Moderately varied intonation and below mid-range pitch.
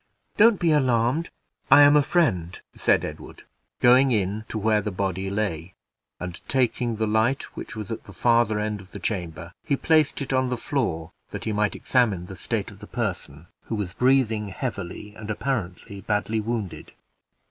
Yes: average, 4.6 semitones; low, 110 Hz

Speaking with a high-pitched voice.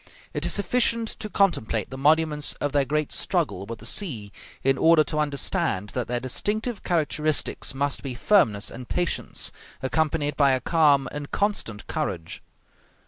No: medium, 145 Hz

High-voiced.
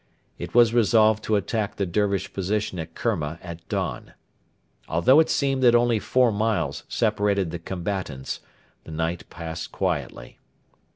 No: low, 100 Hz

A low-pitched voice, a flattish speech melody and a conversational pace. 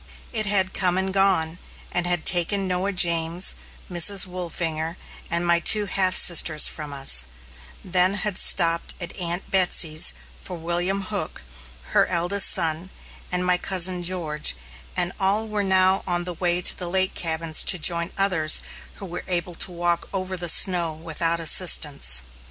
No: medium, 175 Hz; narrow, 2.1 semitones; average, 155 wpm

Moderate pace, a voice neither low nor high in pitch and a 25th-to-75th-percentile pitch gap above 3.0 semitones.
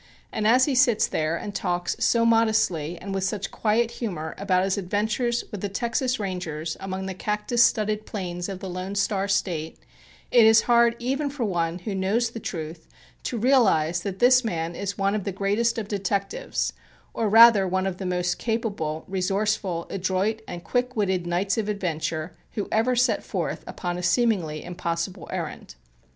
No: average, 175 wpm; high, 195 Hz; average, 4.0 semitones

